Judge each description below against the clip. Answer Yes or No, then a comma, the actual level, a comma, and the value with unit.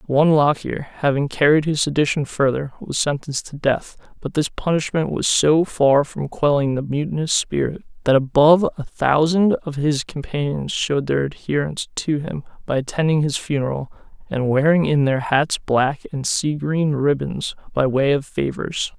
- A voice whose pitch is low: No, medium, 145 Hz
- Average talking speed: Yes, average, 165 wpm